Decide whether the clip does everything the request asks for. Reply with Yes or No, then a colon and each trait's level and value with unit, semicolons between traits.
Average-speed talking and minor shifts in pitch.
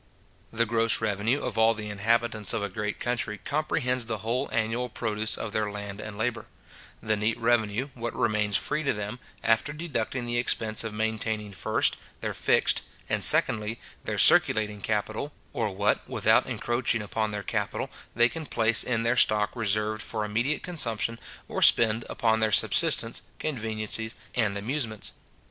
Yes: average, 160 wpm; narrow, 1.9 semitones